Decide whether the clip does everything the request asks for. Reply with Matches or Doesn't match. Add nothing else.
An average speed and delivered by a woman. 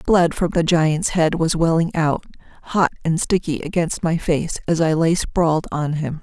Matches